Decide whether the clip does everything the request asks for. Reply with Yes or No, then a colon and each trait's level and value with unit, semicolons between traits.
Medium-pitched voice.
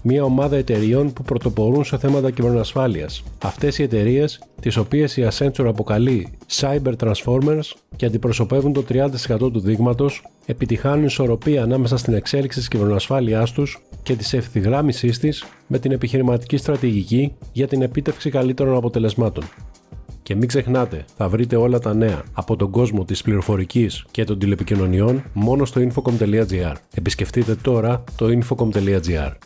No: low, 120 Hz